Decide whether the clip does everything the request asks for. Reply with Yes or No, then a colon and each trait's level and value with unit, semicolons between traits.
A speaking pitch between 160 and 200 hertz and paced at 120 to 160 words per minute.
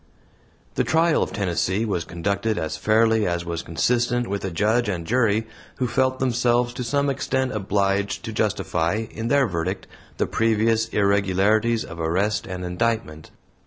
No: low, 110 Hz; average, 155 wpm